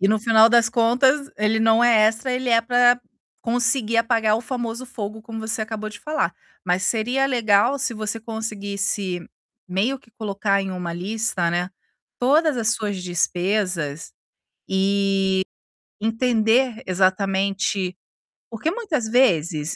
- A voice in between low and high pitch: No, high, 220 Hz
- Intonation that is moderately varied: Yes, average, 3.4 semitones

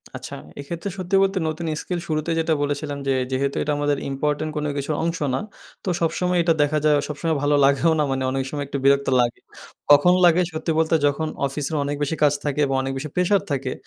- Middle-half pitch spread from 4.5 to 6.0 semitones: No, average, 2.7 semitones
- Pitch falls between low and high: Yes, medium, 150 Hz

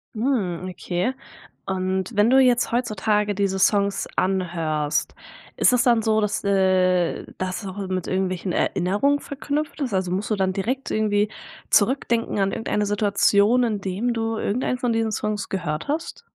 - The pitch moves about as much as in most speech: Yes, average, 3.7 semitones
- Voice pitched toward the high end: Yes, high, 205 Hz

